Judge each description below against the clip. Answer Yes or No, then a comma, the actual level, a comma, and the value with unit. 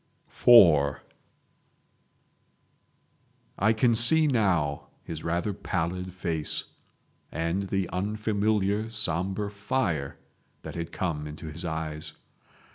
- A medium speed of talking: No, slow, 95 wpm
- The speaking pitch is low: Yes, very low, 90 Hz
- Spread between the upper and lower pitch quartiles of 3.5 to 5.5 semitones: Yes, average, 4.6 semitones